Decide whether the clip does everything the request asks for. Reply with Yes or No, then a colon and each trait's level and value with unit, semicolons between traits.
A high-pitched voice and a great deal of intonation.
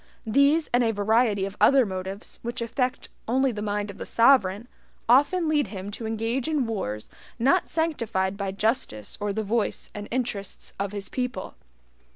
No: high, 225 Hz; average, 4.1 semitones